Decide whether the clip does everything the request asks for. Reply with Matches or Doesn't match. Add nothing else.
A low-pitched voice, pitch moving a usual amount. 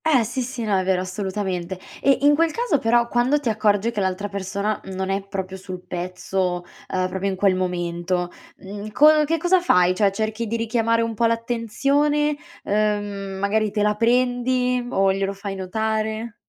Doesn't match